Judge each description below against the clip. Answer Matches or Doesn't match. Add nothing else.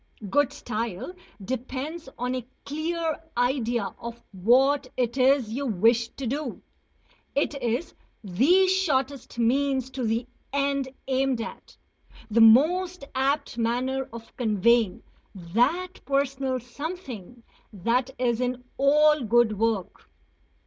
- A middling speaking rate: Doesn't match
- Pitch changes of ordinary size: Matches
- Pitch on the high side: Matches